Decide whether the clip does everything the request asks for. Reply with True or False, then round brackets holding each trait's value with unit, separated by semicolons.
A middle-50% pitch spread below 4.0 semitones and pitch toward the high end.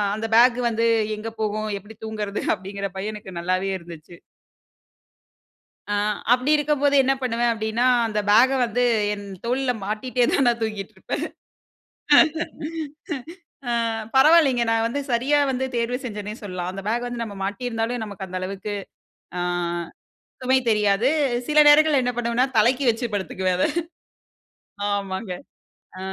True (3.6 semitones; 225 Hz)